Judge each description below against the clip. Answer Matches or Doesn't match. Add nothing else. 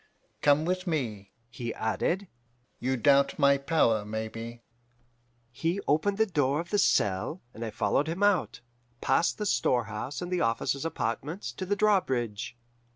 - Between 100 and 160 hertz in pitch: Matches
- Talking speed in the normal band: Matches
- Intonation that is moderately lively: Doesn't match